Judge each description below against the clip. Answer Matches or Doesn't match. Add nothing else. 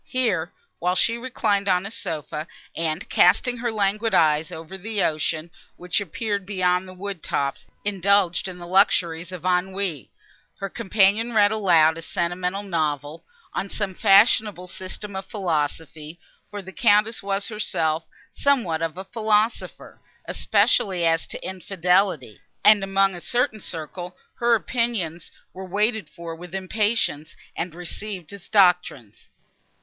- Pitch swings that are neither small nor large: Matches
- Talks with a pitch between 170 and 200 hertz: Matches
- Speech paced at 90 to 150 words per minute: Matches